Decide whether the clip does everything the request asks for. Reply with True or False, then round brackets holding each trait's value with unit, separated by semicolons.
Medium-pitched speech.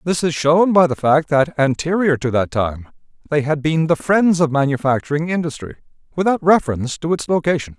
True (155 Hz)